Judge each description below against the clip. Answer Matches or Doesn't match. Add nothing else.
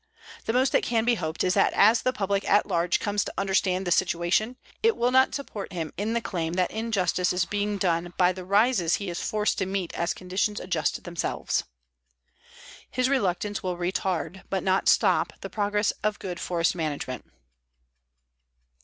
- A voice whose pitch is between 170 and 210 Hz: Matches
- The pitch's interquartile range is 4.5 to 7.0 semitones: Doesn't match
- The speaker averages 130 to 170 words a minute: Doesn't match